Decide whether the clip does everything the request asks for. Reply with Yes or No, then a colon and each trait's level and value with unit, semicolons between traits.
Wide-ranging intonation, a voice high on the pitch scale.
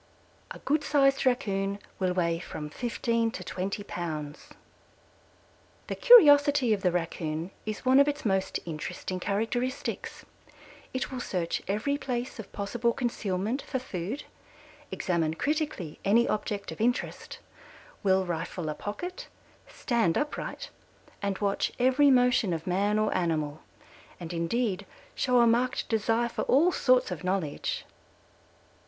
Yes: wide, 5.8 semitones; high, 210 Hz